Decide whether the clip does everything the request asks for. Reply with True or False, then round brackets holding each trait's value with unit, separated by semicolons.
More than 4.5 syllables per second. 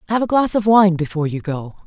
True (6.4 syllables/s)